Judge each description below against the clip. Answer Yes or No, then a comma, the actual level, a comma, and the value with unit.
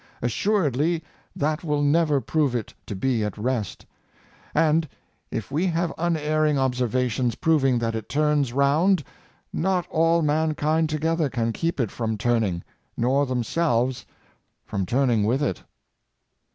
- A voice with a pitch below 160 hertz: Yes, medium, 140 Hz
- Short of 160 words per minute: Yes, average, 140 wpm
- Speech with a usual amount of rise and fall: Yes, average, 4.9 semitones